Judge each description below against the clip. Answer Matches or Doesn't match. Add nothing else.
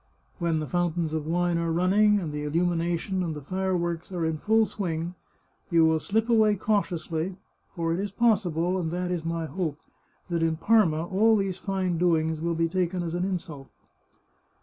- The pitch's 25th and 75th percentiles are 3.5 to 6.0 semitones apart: Doesn't match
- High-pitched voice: Doesn't match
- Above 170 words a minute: Matches